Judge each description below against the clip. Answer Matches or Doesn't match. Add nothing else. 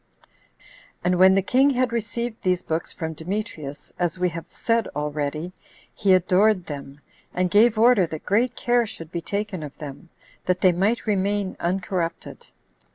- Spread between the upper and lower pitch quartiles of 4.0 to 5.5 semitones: Matches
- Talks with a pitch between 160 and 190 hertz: Matches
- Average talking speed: Matches